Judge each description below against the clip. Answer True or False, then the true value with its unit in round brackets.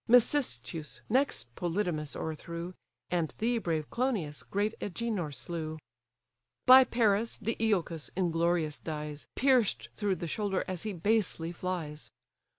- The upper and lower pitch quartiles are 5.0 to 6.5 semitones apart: True (5.6 semitones)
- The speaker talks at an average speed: False (115 wpm)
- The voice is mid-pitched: True (180 Hz)